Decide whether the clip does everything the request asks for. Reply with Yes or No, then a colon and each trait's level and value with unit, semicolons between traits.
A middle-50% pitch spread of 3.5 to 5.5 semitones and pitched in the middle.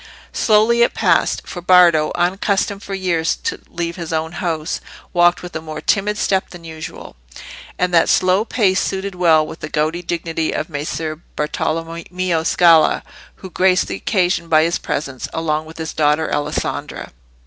No: narrow, 2.6 semitones; medium, 170 Hz